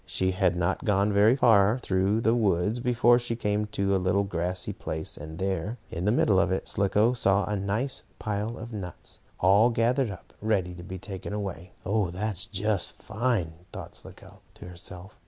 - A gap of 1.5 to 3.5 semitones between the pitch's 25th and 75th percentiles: Yes, average, 2.9 semitones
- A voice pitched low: Yes, low, 100 Hz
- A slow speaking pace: No, average, 185 wpm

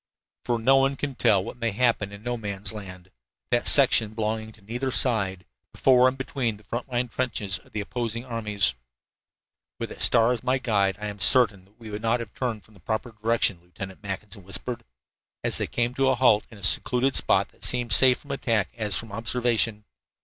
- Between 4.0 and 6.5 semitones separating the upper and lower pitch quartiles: No, average, 3.2 semitones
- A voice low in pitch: Yes, low, 115 Hz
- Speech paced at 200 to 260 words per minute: Yes, fast, 205 wpm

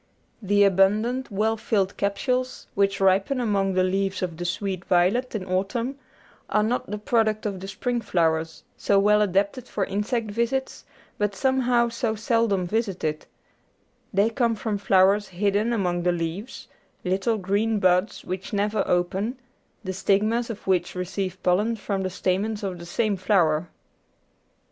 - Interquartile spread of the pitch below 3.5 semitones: Yes, average, 3.1 semitones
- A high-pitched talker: Yes, high, 200 Hz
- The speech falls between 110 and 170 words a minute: Yes, average, 150 wpm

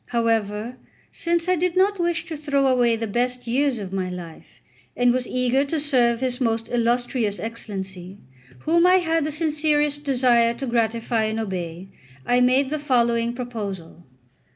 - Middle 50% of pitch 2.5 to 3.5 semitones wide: No, average, 4.5 semitones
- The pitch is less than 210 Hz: No, high, 245 Hz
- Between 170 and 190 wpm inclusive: No, average, 160 wpm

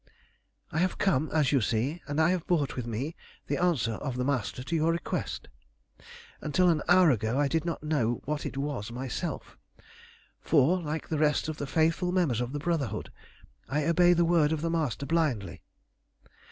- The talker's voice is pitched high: No, medium, 150 Hz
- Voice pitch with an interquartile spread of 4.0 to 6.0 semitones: Yes, average, 4.4 semitones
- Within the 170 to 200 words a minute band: Yes, average, 185 wpm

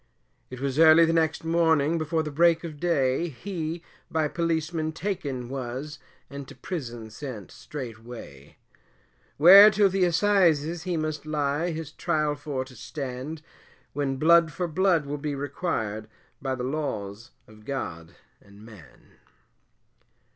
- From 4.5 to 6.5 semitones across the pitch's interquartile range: No, average, 4.1 semitones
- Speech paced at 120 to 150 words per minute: Yes, average, 140 wpm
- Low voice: No, medium, 150 Hz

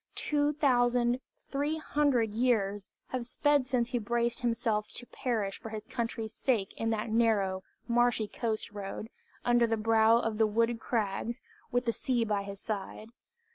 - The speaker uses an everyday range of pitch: No, narrow, 2.2 semitones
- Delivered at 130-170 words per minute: Yes, average, 160 wpm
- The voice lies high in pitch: Yes, high, 230 Hz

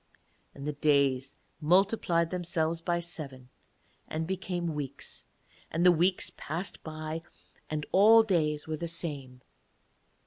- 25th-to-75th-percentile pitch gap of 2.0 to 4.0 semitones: Yes, average, 2.8 semitones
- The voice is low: No, medium, 160 Hz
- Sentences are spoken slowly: Yes, slow, 125 wpm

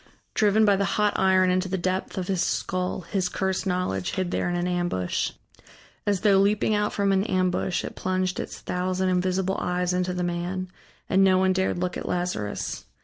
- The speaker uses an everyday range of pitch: No, narrow, 1.1 semitones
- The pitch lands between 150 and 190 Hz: Yes, medium, 185 Hz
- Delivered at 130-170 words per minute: No, average, 195 wpm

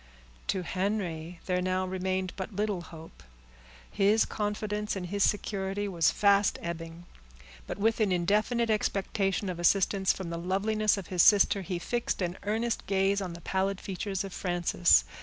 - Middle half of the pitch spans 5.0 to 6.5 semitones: No, narrow, 2.4 semitones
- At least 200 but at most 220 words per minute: No, average, 160 wpm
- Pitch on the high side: Yes, high, 195 Hz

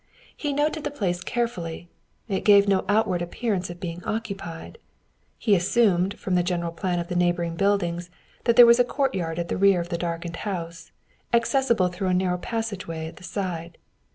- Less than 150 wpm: No, average, 180 wpm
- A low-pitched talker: No, medium, 180 Hz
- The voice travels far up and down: No, average, 4.1 semitones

